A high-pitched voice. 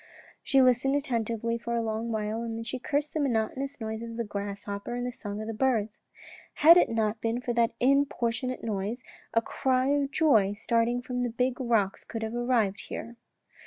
Yes: high, 235 Hz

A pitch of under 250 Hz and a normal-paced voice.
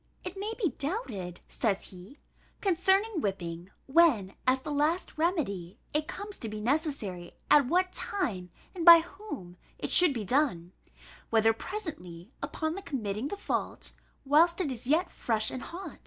No: very high, 285 Hz; average, 155 wpm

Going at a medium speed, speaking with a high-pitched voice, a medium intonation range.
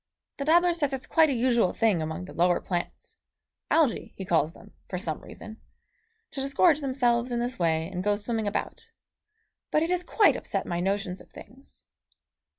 No: average, 180 wpm; high, 235 Hz; wide, 7.3 semitones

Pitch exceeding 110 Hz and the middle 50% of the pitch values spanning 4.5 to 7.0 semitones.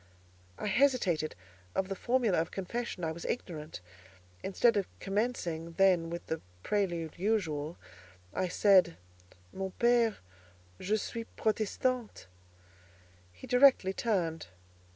Yes: high, 190 Hz; wide, 5.4 semitones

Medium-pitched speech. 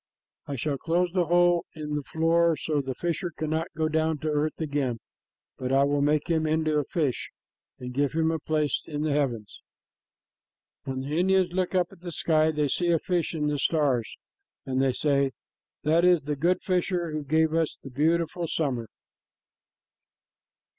Yes: medium, 155 Hz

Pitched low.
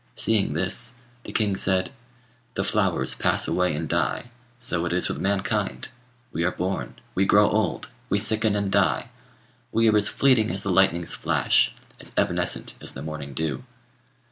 Yes: very low, 95 Hz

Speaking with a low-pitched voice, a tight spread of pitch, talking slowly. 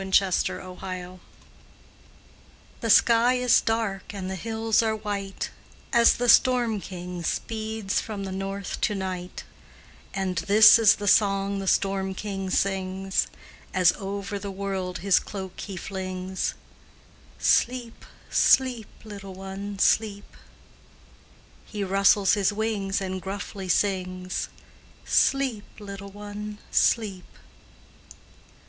No: high, 195 Hz; narrow, 2.1 semitones; slow, 115 wpm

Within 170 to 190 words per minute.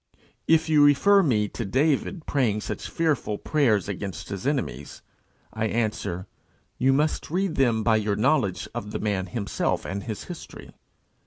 No: average, 155 wpm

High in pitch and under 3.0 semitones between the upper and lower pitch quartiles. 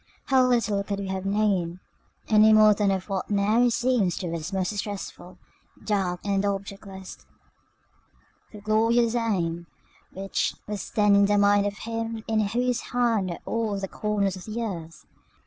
Yes: high, 205 Hz; narrow, 2.4 semitones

